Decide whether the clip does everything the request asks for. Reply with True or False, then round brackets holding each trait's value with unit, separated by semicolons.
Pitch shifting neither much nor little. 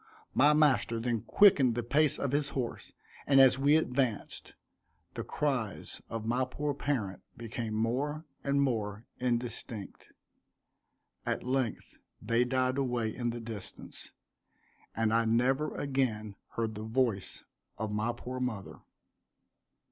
True (3.2 semitones)